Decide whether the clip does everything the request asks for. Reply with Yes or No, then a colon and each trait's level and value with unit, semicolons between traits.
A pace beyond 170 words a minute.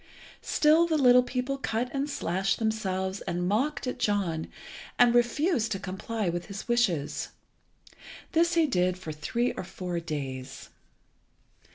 No: average, 140 wpm